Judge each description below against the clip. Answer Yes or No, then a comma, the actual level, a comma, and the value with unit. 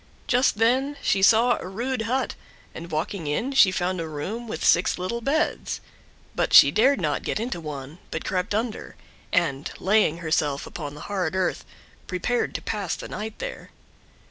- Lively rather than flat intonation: Yes, wide, 6.1 semitones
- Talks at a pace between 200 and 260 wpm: No, average, 170 wpm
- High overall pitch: Yes, high, 195 Hz